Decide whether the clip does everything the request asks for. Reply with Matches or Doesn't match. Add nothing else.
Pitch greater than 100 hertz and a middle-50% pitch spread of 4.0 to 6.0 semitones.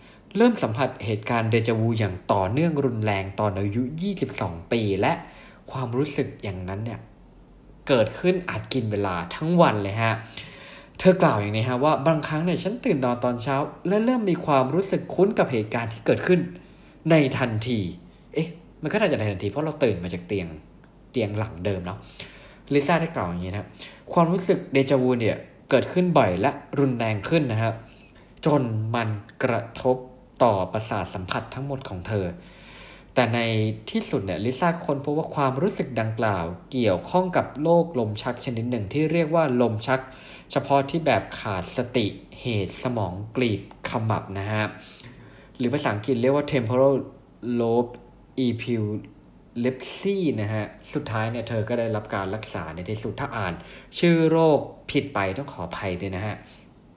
Matches